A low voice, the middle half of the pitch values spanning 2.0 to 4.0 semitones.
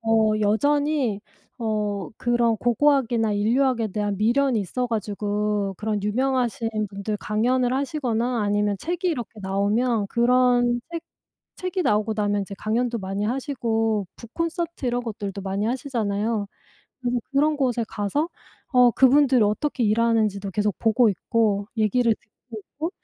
No: high, 225 Hz; average, 3.4 semitones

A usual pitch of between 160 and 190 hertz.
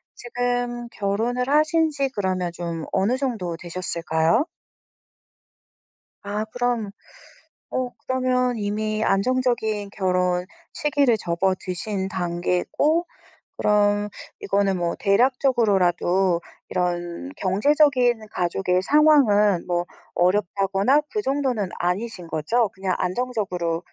No: high, 205 Hz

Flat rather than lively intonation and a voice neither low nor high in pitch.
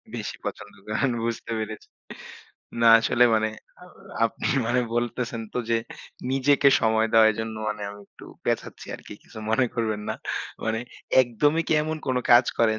No: narrow, 2.2 semitones; low, 115 Hz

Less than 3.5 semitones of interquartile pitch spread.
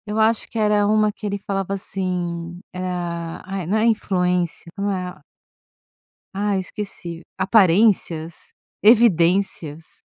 Yes: average, 3.1 semitones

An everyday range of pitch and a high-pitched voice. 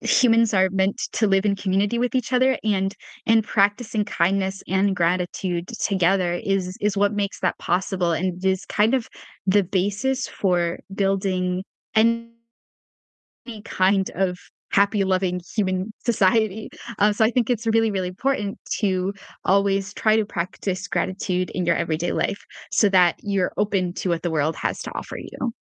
No: narrow, 2.3 semitones; high, 195 Hz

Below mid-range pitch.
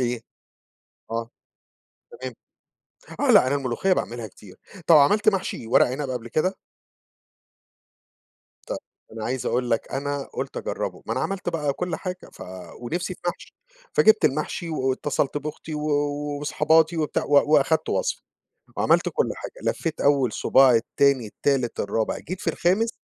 No: medium, 145 Hz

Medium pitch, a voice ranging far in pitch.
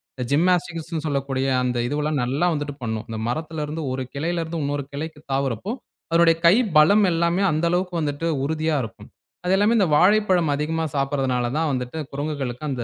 No: medium, 155 Hz; average, 3.4 semitones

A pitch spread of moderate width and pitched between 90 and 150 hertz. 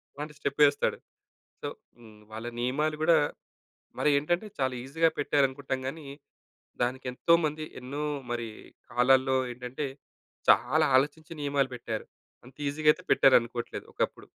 Yes: average, 3.2 semitones; medium, 140 Hz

